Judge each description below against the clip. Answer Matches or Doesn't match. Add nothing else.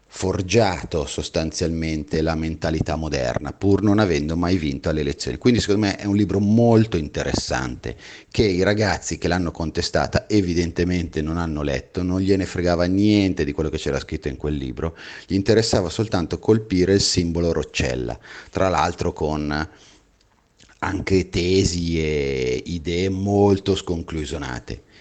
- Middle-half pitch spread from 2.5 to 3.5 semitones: Doesn't match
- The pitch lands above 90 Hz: Doesn't match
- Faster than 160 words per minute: Doesn't match